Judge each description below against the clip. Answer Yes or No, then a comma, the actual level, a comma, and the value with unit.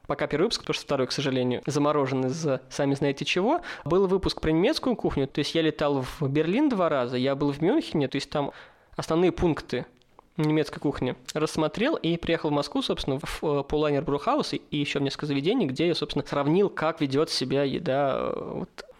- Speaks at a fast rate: Yes, fast, 185 wpm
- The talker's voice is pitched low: No, medium, 150 Hz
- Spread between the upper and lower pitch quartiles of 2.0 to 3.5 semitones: Yes, average, 2.9 semitones